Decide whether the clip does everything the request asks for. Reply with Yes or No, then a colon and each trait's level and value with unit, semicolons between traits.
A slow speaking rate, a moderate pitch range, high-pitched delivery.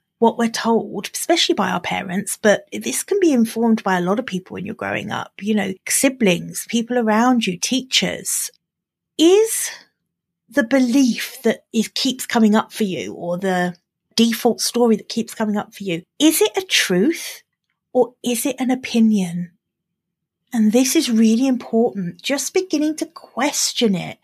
No: average, 165 wpm; average, 5.0 semitones; high, 230 Hz